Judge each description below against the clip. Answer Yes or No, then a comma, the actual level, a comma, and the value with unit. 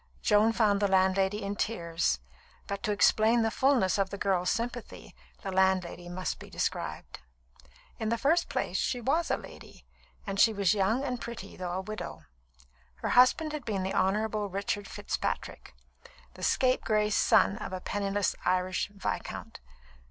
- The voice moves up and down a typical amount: Yes, average, 3.1 semitones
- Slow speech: No, average, 160 wpm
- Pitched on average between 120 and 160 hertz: No, high, 205 Hz